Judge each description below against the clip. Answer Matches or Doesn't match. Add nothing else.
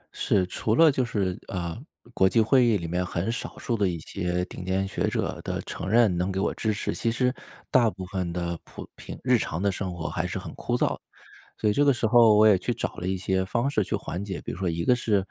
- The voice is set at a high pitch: Doesn't match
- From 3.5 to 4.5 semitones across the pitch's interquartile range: Matches